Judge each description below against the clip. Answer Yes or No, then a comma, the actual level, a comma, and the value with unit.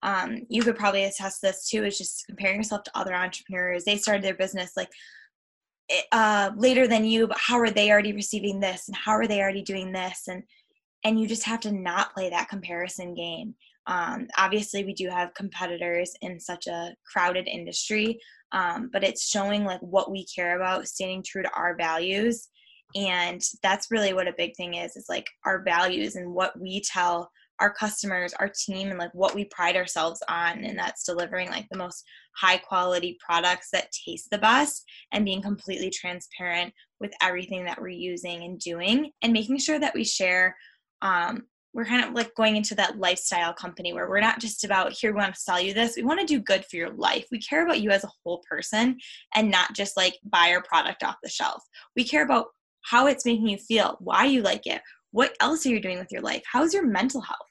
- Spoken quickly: Yes, fast, 210 wpm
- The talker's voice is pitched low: No, high, 195 Hz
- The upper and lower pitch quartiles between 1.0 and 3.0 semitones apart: No, average, 3.5 semitones